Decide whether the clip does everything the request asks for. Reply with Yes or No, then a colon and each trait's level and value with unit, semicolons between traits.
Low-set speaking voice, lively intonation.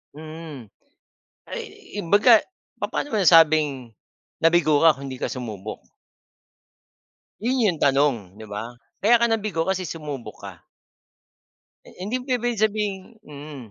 No: medium, 160 Hz; wide, 7.3 semitones